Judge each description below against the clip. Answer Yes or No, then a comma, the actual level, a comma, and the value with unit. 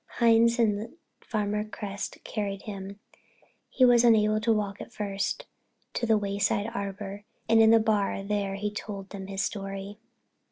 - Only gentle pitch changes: Yes, narrow, 2.0 semitones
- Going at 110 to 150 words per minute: Yes, average, 145 wpm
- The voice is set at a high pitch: Yes, high, 210 Hz